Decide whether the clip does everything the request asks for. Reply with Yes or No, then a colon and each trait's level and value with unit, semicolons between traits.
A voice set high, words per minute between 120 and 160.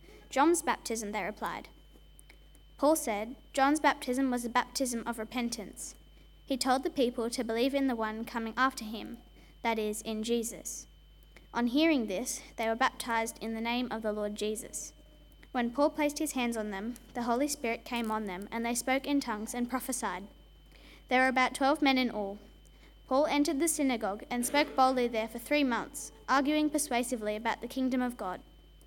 No: high, 245 Hz; average, 180 wpm